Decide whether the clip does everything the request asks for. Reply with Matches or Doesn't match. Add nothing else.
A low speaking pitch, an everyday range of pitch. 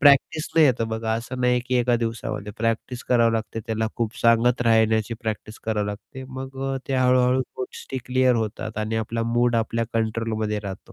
Doesn't match